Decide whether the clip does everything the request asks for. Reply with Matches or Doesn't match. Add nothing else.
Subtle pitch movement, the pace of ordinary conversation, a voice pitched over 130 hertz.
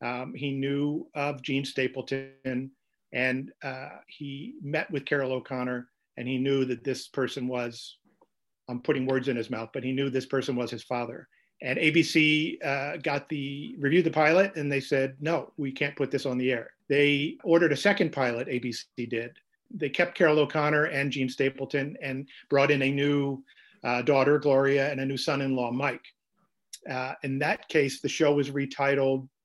Matches